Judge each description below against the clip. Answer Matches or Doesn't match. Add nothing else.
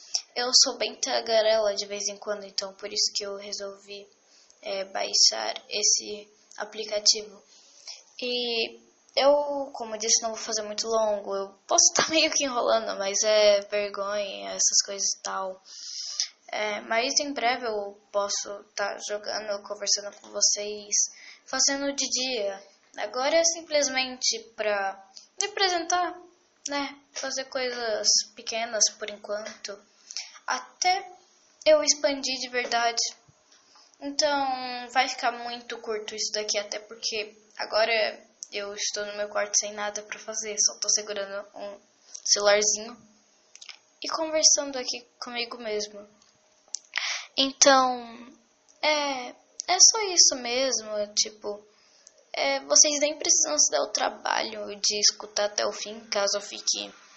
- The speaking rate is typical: Doesn't match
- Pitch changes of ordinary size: Matches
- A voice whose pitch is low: Doesn't match